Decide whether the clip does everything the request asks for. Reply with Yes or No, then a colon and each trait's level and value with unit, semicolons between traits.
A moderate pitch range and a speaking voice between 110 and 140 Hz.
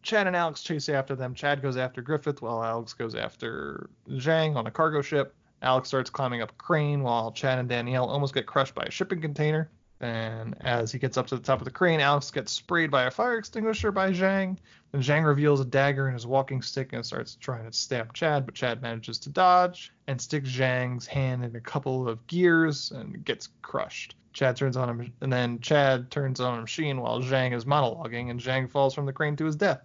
Yes: average, 3.3 semitones; low, 135 Hz